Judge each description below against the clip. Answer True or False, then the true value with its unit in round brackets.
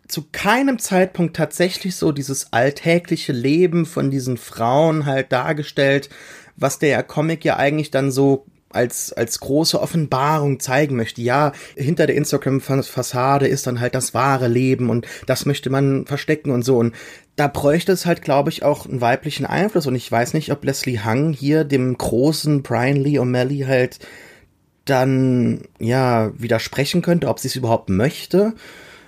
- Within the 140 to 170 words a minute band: True (160 wpm)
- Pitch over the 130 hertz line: True (140 Hz)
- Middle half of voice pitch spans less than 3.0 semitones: False (3.3 semitones)